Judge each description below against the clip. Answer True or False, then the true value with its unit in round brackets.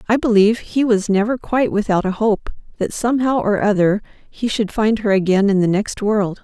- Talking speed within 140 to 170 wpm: False (205 wpm)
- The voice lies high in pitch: True (210 Hz)